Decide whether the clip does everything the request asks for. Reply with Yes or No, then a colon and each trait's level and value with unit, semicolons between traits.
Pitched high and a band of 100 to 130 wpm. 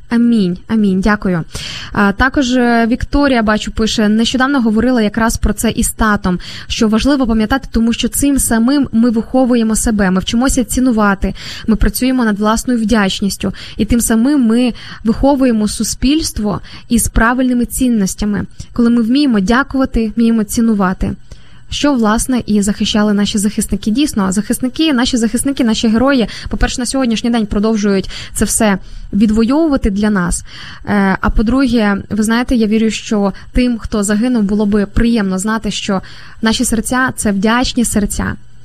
No: high, 225 Hz; average, 140 wpm